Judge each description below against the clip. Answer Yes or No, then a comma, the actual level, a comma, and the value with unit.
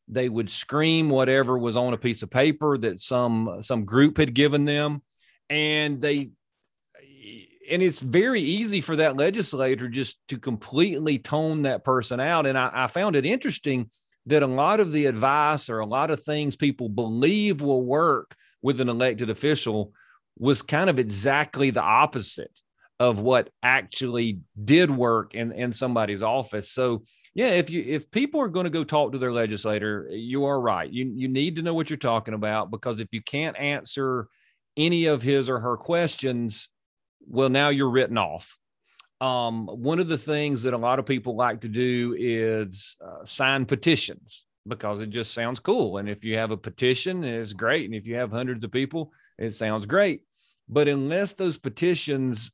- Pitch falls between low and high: No, low, 130 Hz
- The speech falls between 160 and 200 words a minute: Yes, average, 180 wpm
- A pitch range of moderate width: Yes, average, 4.2 semitones